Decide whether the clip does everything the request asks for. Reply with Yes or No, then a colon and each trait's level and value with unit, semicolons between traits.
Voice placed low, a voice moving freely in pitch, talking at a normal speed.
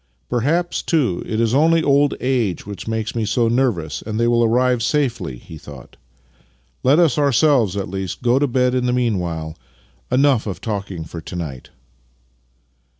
Yes: low, 115 Hz; wide, 5.9 semitones; average, 175 wpm